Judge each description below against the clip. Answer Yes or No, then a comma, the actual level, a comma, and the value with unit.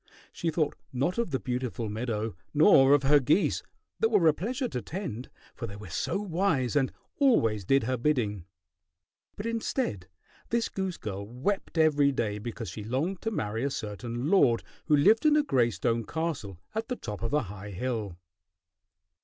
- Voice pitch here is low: Yes, low, 130 Hz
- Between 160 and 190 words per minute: Yes, average, 180 wpm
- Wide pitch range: Yes, wide, 8.0 semitones